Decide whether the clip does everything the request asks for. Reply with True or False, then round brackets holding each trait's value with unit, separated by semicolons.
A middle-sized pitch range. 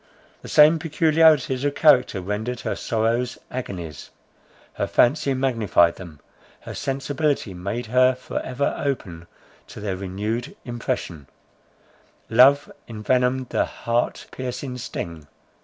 True (4.8 semitones)